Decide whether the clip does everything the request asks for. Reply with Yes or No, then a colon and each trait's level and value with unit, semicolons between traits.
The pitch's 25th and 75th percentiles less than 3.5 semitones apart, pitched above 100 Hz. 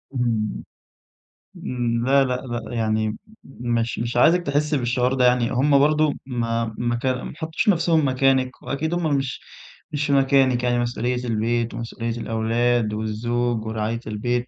Yes: narrow, 2.6 semitones; low, 120 Hz